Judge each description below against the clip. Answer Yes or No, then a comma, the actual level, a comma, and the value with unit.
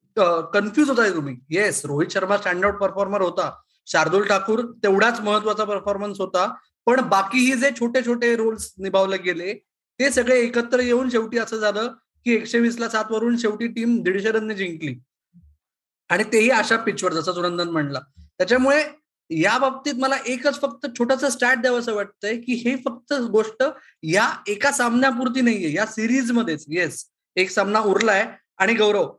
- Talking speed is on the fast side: Yes, fast, 160 wpm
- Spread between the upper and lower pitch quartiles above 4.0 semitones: Yes, average, 4.5 semitones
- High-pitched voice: Yes, high, 220 Hz